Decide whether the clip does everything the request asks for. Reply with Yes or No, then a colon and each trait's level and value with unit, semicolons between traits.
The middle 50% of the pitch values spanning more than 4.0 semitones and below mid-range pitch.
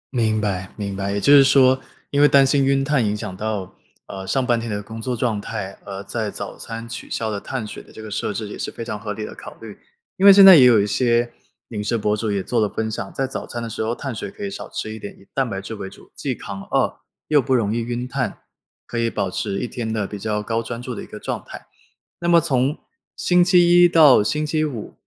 Yes: average, 4.4 semitones; low, 115 Hz